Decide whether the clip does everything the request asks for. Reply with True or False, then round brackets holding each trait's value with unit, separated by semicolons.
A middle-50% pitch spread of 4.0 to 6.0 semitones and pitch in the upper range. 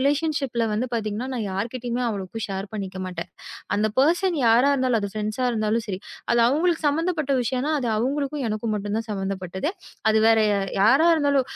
True (4.9 semitones; 235 Hz)